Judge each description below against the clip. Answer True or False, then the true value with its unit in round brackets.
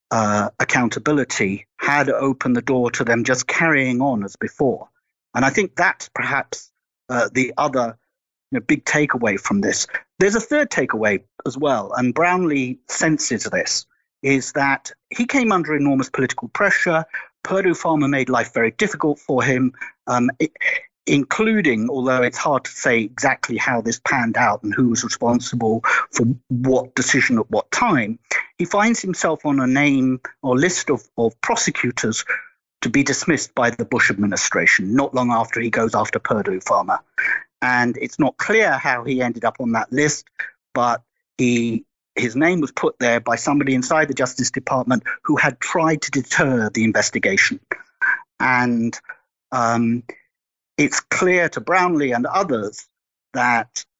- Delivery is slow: False (160 wpm)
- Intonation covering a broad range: True (5.9 semitones)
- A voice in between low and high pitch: False (130 Hz)